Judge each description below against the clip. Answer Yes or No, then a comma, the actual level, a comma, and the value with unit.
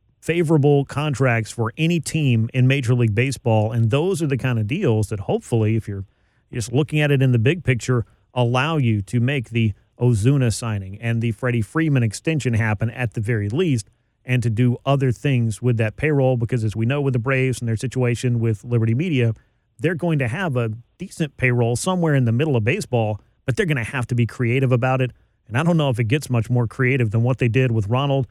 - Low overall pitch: Yes, low, 125 Hz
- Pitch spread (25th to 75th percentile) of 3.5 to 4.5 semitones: No, average, 2.9 semitones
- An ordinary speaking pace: No, fast, 225 wpm